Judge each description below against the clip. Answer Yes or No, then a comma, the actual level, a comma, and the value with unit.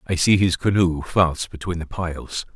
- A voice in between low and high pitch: No, very low, 85 Hz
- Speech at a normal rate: Yes, average, 190 wpm